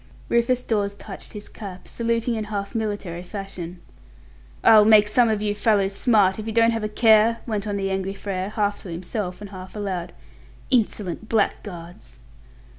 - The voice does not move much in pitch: Yes, narrow, 2.3 semitones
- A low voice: No, high, 205 Hz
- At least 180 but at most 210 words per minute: No, average, 155 wpm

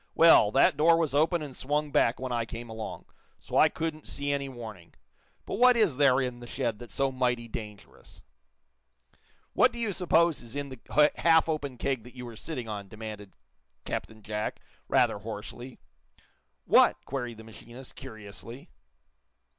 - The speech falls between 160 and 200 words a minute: Yes, average, 165 wpm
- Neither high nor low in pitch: No, low, 125 Hz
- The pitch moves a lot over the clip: No, average, 4.8 semitones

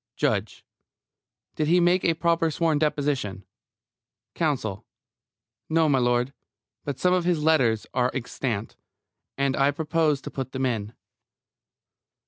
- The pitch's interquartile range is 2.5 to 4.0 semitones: No, average, 4.5 semitones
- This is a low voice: No, medium, 145 Hz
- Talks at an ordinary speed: No, slow, 120 wpm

